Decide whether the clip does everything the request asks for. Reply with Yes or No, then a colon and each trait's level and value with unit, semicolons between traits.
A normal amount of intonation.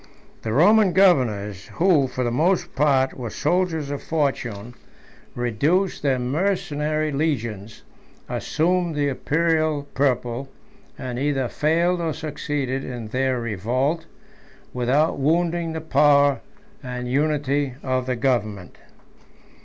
Yes: average, 4.2 semitones